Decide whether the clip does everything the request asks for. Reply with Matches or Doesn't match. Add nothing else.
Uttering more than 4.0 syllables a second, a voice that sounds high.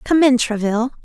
Matches